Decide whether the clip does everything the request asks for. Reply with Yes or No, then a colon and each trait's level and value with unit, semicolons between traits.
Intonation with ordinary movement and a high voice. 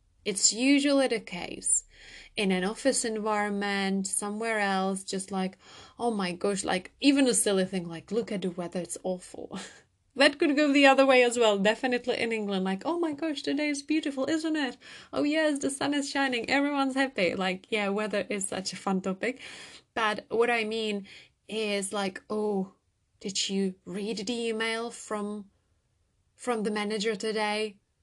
Yes: average, 4.7 semitones; high, 215 Hz